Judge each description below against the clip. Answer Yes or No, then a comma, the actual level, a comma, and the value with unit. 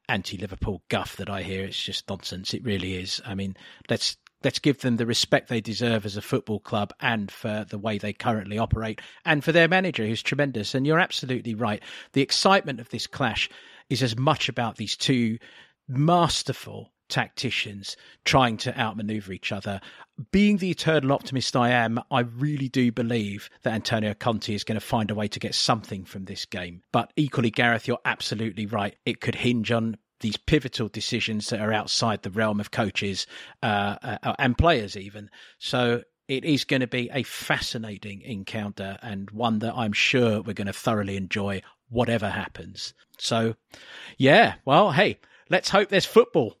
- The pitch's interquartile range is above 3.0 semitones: Yes, average, 3.6 semitones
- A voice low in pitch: Yes, low, 115 Hz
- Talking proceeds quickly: No, average, 180 wpm